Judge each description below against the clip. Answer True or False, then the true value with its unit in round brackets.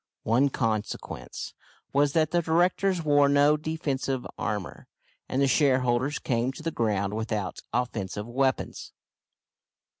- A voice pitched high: False (135 Hz)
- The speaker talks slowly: True (120 wpm)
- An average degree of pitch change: True (4.4 semitones)